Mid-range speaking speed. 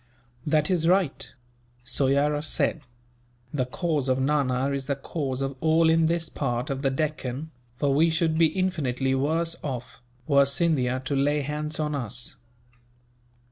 Yes: average, 150 wpm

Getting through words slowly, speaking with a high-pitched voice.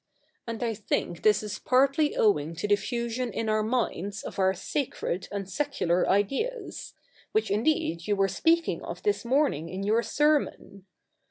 No: average, 165 wpm; high, 215 Hz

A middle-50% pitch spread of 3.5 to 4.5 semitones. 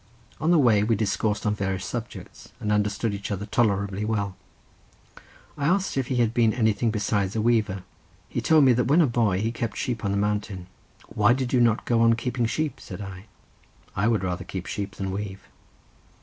No: average, 3.0 semitones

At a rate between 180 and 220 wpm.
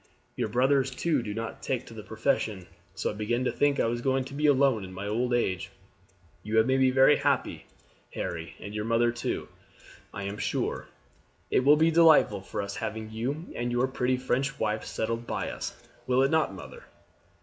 Yes: average, 200 wpm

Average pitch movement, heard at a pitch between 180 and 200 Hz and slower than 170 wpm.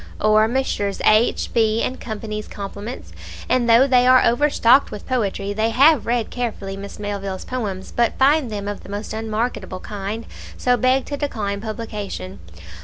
No: average, 3.5 semitones; high, 220 Hz; average, 160 wpm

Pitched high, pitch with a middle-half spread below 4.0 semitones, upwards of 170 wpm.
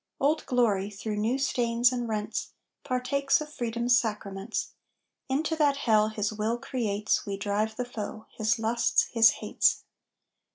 No: high, 230 Hz; average, 2.9 semitones; average, 140 wpm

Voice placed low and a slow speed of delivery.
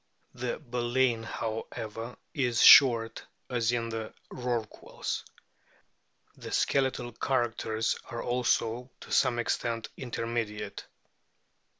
Yes: low, 120 Hz; slow, 90 wpm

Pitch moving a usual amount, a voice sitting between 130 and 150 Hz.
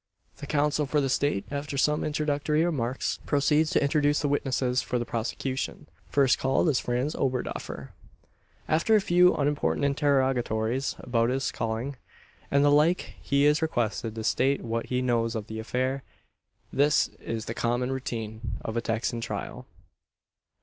Yes: average, 3.7 semitones; low, 135 Hz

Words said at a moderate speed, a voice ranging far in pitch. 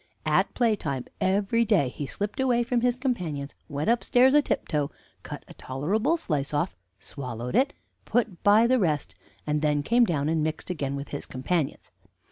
Yes: average, 170 wpm; wide, 8.6 semitones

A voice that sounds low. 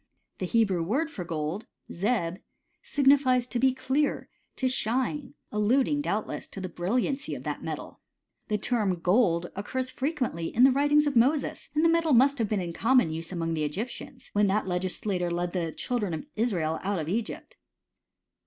No: high, 220 Hz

